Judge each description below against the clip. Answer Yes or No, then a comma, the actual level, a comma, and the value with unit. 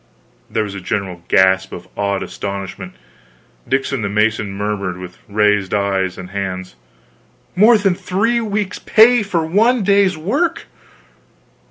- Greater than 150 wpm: No, slow, 135 wpm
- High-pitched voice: No, low, 105 Hz